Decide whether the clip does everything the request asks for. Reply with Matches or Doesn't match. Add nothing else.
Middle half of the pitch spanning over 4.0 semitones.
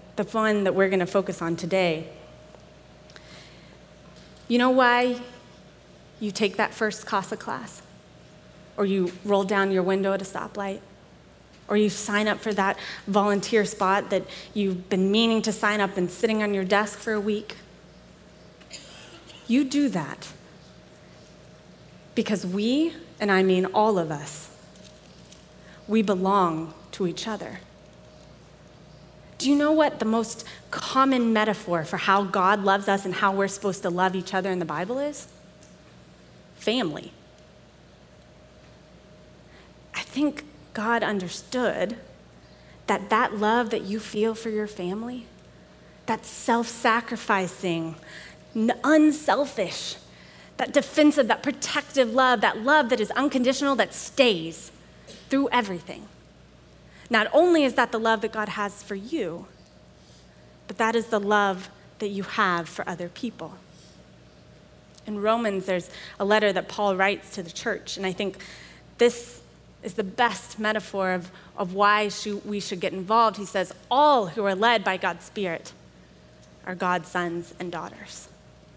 Doesn't match